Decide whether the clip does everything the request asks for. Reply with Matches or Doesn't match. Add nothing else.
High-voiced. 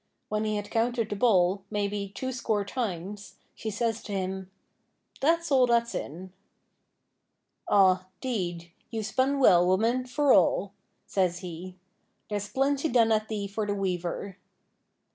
Matches